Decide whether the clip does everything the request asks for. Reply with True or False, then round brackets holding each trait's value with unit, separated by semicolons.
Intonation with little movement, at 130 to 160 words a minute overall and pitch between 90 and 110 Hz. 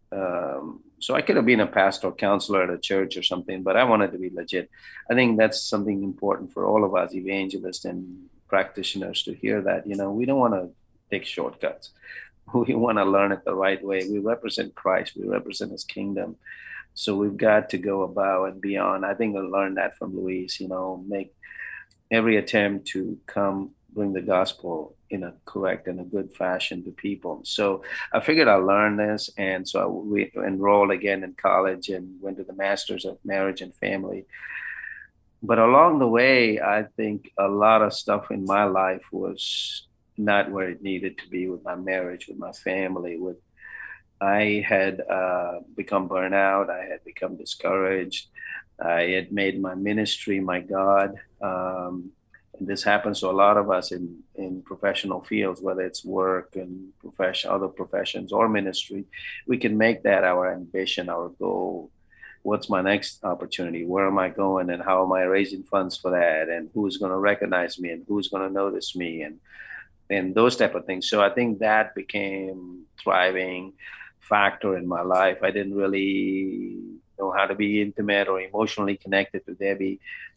False (1.5 semitones; 185 wpm; 95 Hz)